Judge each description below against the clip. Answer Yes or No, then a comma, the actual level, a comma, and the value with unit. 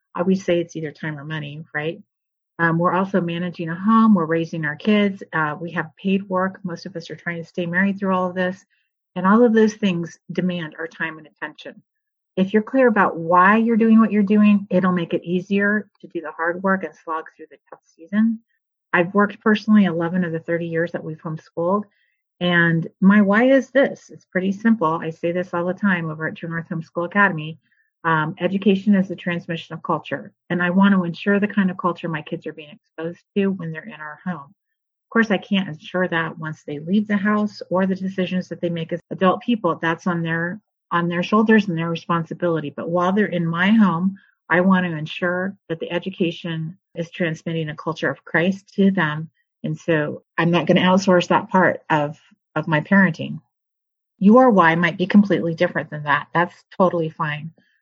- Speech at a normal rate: No, fast, 210 wpm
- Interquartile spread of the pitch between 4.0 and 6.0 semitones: No, average, 3.0 semitones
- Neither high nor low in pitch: Yes, medium, 175 Hz